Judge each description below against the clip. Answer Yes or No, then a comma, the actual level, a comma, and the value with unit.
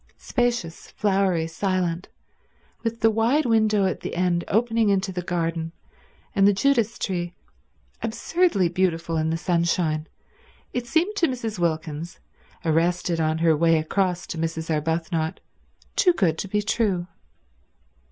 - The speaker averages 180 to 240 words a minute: No, slow, 135 wpm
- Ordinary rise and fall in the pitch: Yes, average, 4.8 semitones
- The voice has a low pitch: No, medium, 180 Hz